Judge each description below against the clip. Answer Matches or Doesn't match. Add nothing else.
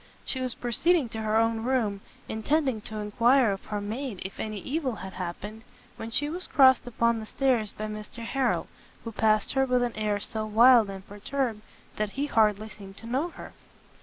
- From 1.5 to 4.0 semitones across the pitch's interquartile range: Matches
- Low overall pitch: Doesn't match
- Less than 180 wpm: Doesn't match